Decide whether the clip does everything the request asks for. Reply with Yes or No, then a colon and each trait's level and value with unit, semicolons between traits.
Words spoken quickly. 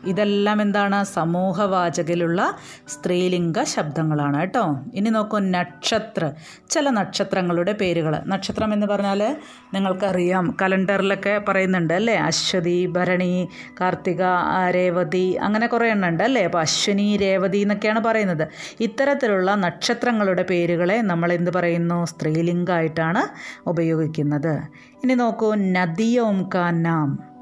No: average, 95 wpm